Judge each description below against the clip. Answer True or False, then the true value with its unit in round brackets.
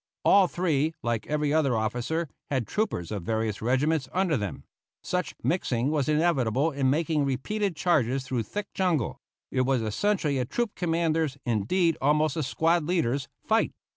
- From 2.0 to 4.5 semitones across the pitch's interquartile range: False (5.0 semitones)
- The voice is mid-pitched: True (150 Hz)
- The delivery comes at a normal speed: True (155 wpm)